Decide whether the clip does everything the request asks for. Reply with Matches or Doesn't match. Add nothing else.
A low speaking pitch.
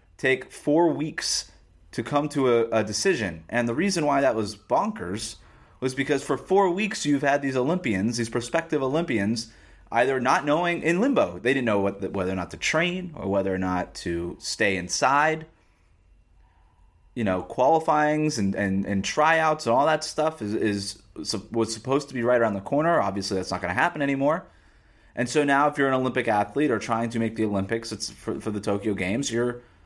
Matches